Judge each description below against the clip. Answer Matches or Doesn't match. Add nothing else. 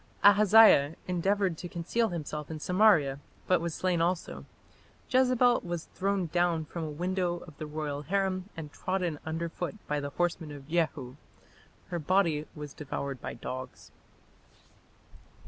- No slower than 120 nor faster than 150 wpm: Matches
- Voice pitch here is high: Doesn't match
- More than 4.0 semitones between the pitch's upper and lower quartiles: Doesn't match